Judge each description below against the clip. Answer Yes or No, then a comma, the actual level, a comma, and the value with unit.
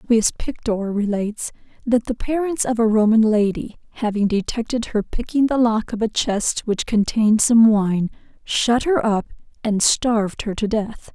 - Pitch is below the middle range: No, high, 225 Hz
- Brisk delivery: No, average, 165 wpm